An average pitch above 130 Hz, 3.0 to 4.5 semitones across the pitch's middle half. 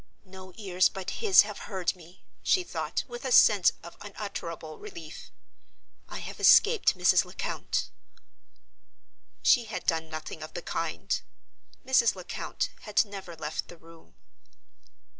Yes: medium, 185 Hz; average, 4.2 semitones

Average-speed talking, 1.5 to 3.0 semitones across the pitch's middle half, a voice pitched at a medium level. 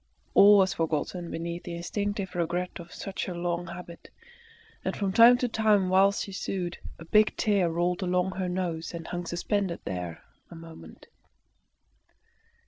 Yes: average, 155 wpm; narrow, 2.5 semitones; medium, 180 Hz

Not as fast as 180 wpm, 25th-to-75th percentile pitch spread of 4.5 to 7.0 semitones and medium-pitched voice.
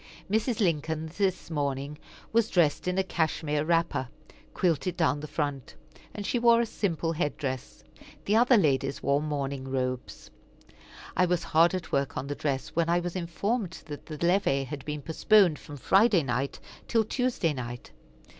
Yes: average, 165 wpm; average, 5.0 semitones; medium, 160 Hz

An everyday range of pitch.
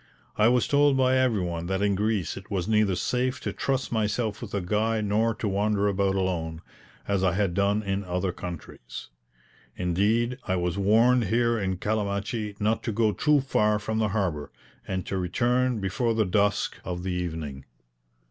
Yes: average, 3.3 semitones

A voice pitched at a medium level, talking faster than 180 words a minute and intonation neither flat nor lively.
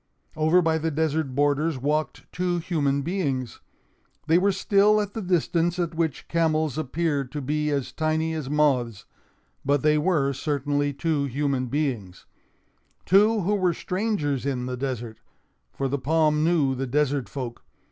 No: medium, 150 Hz; average, 150 wpm; average, 3.3 semitones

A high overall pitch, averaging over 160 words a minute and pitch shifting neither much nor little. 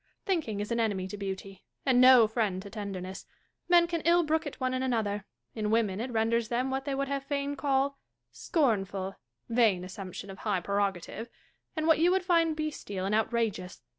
No: high, 230 Hz; average, 195 wpm; wide, 5.8 semitones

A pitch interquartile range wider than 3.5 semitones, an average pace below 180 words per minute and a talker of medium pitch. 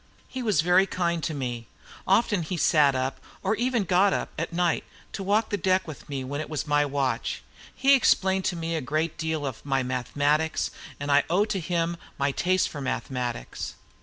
No: average, 4.8 semitones; average, 195 wpm; medium, 160 Hz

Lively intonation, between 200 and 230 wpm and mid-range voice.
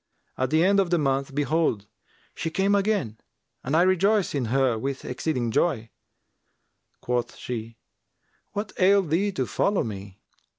No: wide, 7.5 semitones; average, 145 wpm; medium, 145 Hz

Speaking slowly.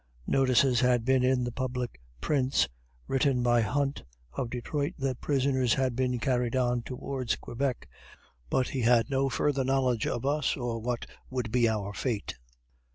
No: average, 160 wpm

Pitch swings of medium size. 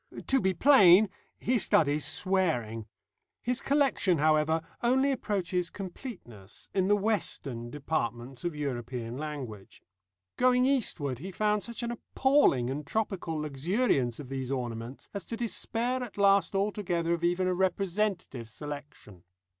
No: wide, 7.7 semitones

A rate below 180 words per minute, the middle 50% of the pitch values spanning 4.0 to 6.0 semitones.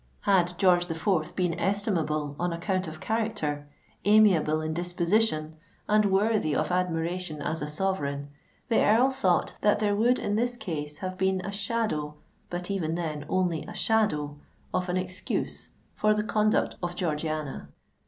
Yes: average, 150 wpm; average, 4.7 semitones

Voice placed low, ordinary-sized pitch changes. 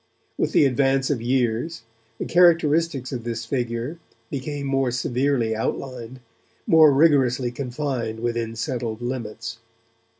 Yes: low, 125 Hz; average, 3.2 semitones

